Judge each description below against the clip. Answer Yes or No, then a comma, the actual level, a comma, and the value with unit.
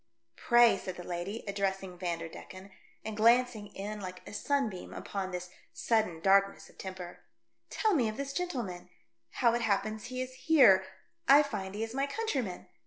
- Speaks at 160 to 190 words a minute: Yes, average, 175 wpm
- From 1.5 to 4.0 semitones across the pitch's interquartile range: No, average, 4.8 semitones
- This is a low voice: No, high, 205 Hz